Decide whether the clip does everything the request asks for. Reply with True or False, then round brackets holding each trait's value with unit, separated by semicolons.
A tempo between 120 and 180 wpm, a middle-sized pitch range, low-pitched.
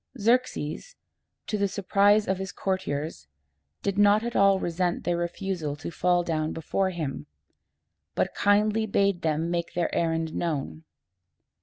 False (140 wpm; 3.6 semitones; 180 Hz)